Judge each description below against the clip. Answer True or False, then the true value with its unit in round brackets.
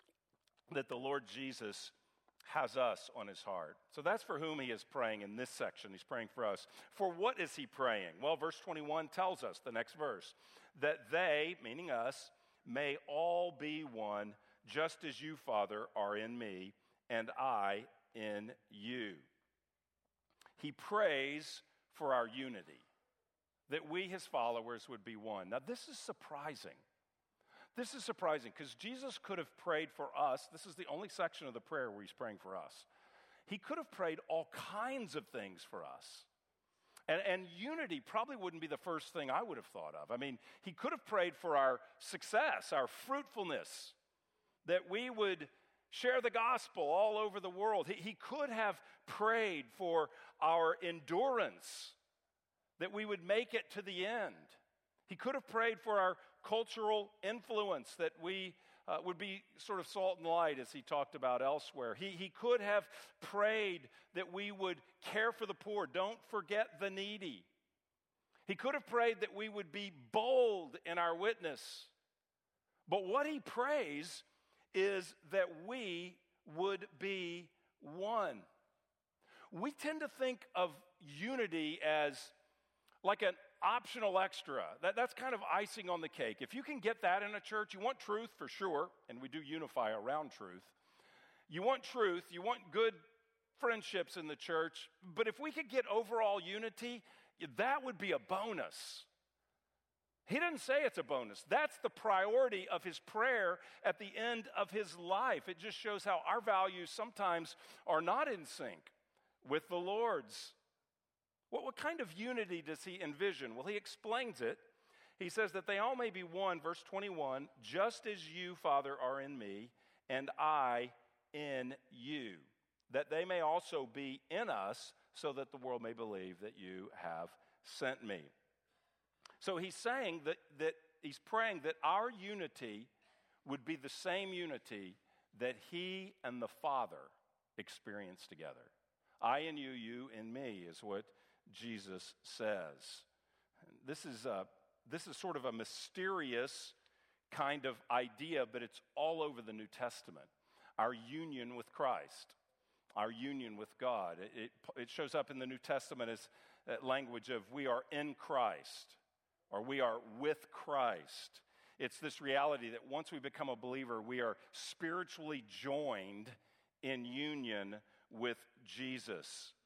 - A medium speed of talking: True (160 wpm)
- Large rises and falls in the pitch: True (8.0 semitones)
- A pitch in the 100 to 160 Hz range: False (175 Hz)